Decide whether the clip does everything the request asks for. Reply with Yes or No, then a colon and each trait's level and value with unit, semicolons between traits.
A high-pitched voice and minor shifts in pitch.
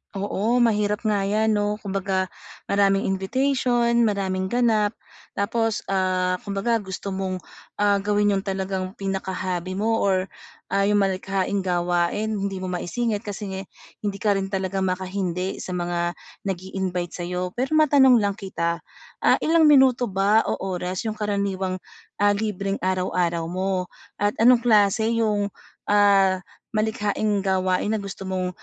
Yes: high, 195 Hz; narrow, 2.0 semitones